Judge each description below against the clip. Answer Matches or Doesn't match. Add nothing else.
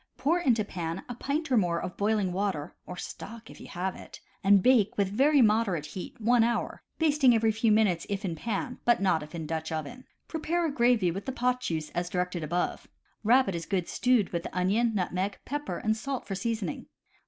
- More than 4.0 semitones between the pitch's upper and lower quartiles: Matches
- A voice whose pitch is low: Doesn't match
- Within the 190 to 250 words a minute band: Matches